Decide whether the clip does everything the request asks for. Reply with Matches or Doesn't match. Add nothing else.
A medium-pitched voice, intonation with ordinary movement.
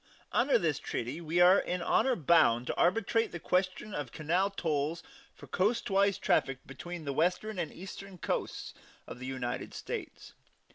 Matches